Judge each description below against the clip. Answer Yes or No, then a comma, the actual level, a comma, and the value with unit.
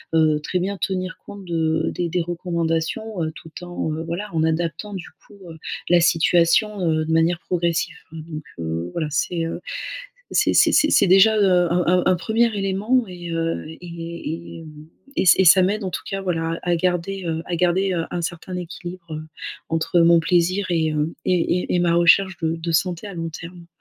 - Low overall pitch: No, medium, 170 Hz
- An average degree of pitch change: No, narrow, 2.0 semitones